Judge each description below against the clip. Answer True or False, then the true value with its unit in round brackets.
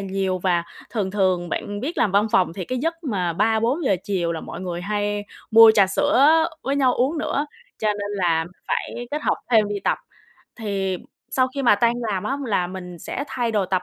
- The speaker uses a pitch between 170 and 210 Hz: True (205 Hz)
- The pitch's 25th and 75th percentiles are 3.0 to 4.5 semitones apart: False (4.9 semitones)